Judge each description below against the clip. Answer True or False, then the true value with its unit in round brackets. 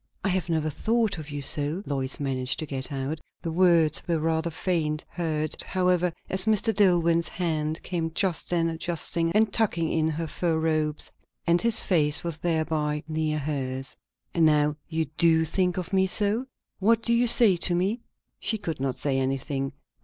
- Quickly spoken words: False (175 wpm)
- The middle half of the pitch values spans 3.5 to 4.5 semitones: False (3.1 semitones)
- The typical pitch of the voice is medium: True (165 Hz)